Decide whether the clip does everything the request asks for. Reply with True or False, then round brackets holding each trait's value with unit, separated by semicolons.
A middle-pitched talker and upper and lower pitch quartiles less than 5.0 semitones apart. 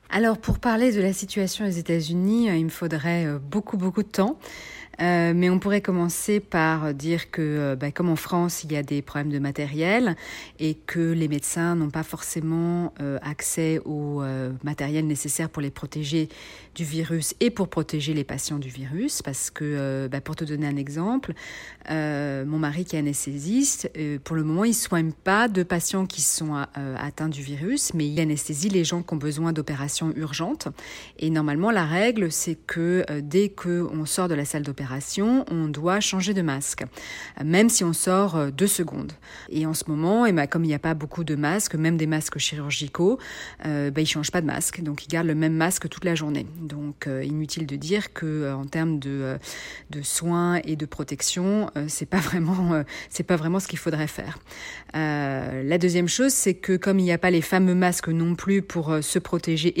True (160 Hz; 3.3 semitones)